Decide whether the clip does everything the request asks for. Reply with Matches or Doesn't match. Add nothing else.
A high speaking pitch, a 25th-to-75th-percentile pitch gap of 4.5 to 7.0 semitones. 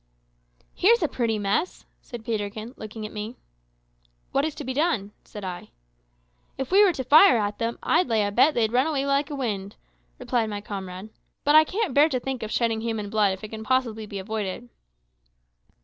Matches